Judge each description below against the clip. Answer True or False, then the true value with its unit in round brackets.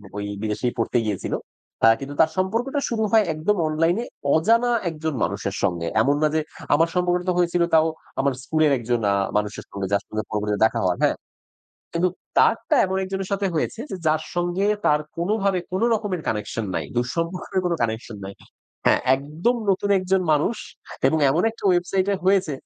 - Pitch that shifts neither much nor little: False (7.4 semitones)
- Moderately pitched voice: True (165 Hz)